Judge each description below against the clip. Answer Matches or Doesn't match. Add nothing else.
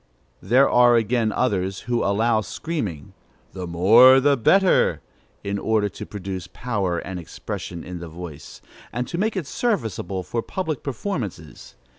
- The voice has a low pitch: Matches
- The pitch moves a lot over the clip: Matches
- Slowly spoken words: Doesn't match